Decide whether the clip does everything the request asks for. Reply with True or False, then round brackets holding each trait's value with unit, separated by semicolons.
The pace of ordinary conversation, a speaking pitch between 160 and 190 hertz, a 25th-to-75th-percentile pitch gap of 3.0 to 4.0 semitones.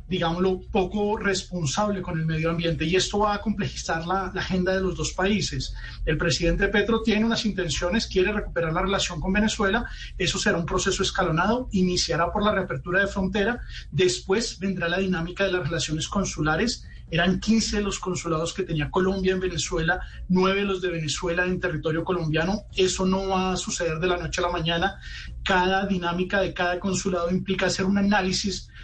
False (180 wpm; 185 Hz; 2.4 semitones)